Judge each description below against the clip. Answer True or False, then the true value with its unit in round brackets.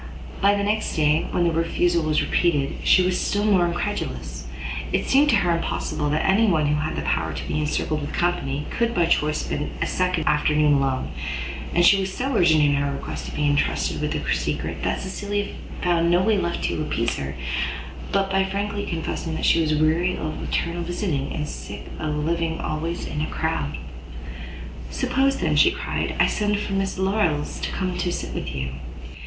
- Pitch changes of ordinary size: True (4.3 semitones)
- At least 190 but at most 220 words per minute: True (195 wpm)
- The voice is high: False (170 Hz)